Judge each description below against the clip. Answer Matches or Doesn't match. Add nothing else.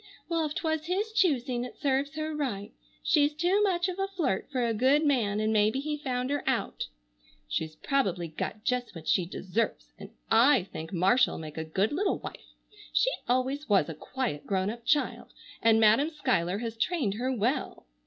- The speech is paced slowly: Doesn't match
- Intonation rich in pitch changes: Matches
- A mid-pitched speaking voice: Doesn't match